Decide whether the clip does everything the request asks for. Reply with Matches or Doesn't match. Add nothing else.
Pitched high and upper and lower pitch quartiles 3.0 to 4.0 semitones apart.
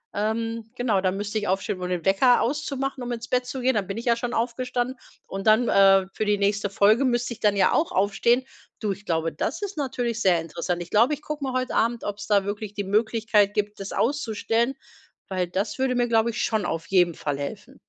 Matches